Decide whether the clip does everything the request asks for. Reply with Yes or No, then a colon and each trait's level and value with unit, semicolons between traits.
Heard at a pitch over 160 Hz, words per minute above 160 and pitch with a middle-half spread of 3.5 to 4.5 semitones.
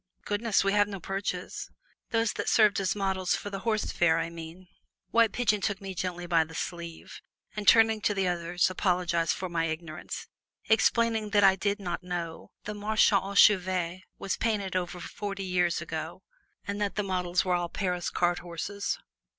No: high, 190 Hz; average, 180 wpm; average, 2.8 semitones